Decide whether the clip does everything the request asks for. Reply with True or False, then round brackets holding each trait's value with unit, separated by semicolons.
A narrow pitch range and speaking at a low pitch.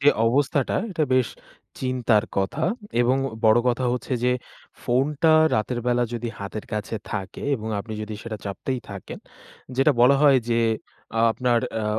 False (3.3 semitones; 120 Hz)